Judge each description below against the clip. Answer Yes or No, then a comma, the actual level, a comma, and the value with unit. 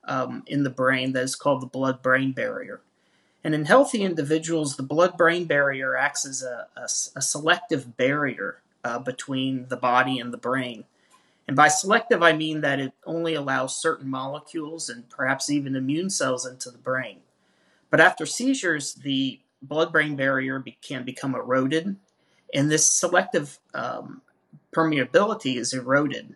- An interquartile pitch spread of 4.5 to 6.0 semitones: No, average, 3.4 semitones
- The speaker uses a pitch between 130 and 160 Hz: Yes, medium, 140 Hz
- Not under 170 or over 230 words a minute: No, average, 155 wpm